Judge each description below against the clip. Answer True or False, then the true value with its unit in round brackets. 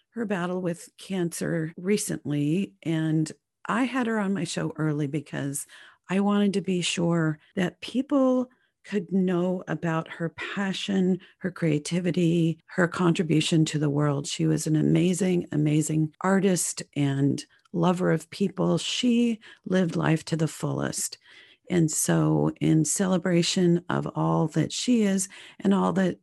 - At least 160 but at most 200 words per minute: False (140 wpm)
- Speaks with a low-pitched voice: False (175 Hz)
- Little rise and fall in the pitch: False (3.5 semitones)